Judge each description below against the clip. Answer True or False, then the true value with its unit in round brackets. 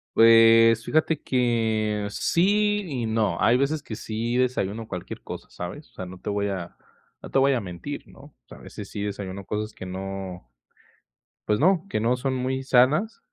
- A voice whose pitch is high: False (115 Hz)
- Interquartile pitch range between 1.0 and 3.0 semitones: False (4.7 semitones)